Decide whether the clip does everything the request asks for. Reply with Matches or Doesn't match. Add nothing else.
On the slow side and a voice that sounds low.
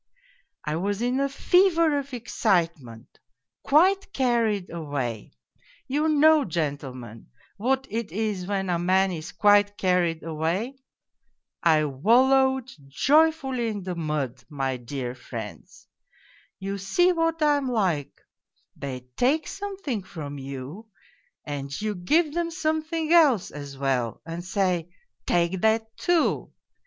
Doesn't match